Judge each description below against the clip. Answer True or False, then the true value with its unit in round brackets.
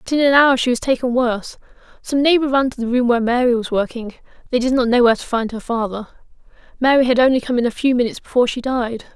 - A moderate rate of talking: False (250 wpm)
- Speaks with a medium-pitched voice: False (245 Hz)